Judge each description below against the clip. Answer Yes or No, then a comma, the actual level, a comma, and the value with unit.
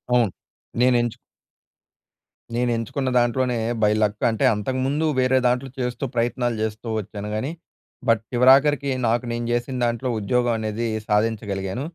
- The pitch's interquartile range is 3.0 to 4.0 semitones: No, narrow, 2.6 semitones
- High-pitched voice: No, low, 120 Hz